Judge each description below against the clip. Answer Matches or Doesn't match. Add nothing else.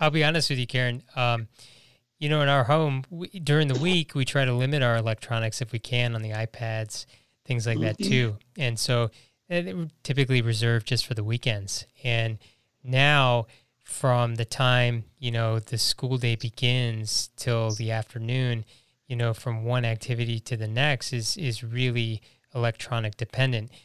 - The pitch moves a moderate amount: Doesn't match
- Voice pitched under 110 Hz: Doesn't match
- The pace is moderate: Matches